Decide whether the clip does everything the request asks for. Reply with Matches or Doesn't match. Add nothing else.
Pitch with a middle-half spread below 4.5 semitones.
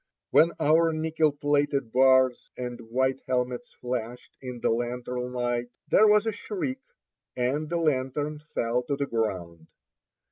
Matches